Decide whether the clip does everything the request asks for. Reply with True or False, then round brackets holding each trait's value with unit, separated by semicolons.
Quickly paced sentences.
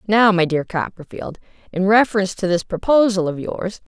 False (165 wpm)